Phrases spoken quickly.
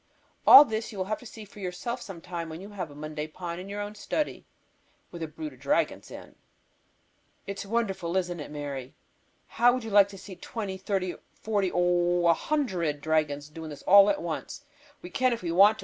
Yes: fast, 215 wpm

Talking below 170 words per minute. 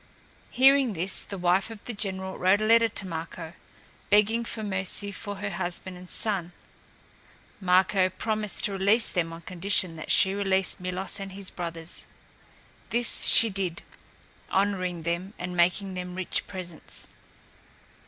Yes: average, 145 wpm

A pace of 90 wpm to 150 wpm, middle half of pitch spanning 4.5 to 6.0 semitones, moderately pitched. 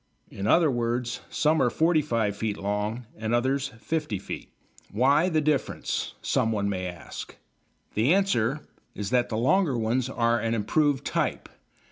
No: average, 145 wpm; average, 5.2 semitones; low, 120 Hz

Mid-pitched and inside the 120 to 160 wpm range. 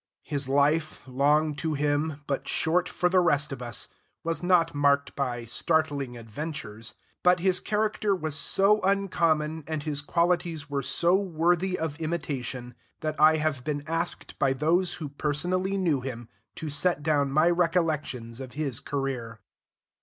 Yes: medium, 155 Hz; average, 155 wpm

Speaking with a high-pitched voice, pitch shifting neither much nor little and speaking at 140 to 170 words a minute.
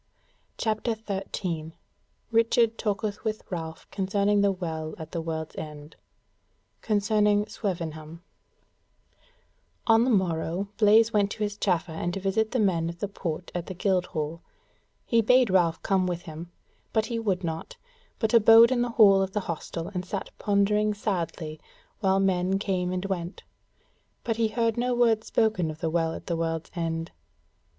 Yes: high, 195 Hz; average, 4.3 semitones; average, 160 wpm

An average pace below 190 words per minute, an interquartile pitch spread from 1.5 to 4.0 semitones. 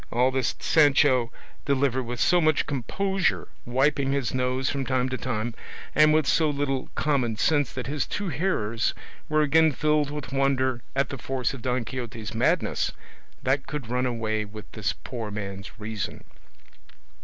Yes: average, 160 wpm; average, 3.5 semitones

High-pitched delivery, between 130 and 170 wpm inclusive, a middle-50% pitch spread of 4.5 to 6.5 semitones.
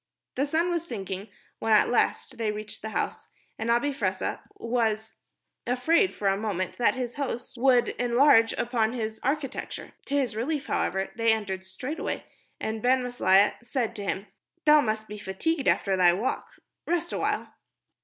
No: high, 230 Hz; average, 165 wpm; average, 4.0 semitones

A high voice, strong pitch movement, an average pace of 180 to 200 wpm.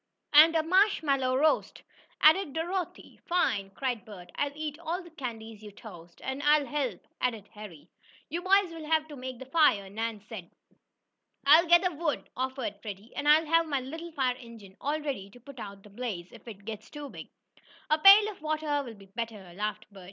Yes: very high, 265 Hz; wide, 6.6 semitones; average, 190 wpm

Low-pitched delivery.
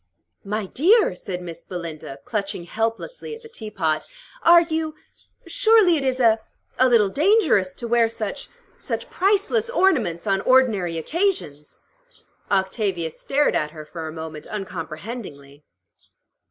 No: high, 215 Hz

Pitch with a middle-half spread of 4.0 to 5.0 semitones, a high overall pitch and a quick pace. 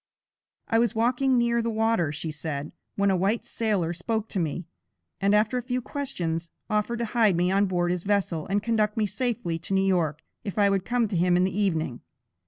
Yes: average, 4.5 semitones; high, 200 Hz; fast, 210 wpm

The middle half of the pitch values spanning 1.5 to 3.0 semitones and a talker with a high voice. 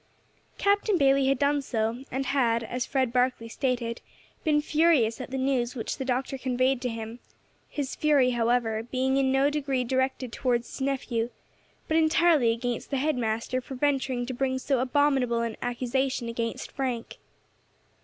Yes: narrow, 2.4 semitones; very high, 260 Hz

